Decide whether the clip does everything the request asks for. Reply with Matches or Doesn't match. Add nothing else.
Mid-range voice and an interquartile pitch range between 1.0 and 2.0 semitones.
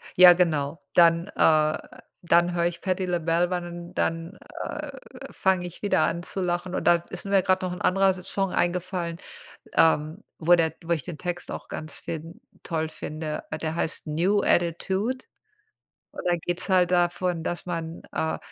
Matches